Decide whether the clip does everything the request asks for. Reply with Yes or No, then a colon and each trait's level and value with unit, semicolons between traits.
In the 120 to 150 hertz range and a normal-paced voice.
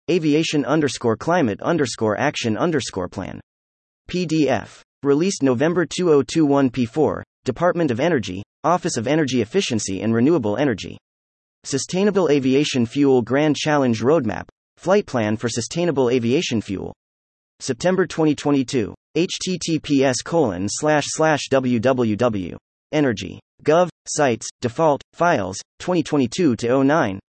No: low, 135 Hz; slow, 100 wpm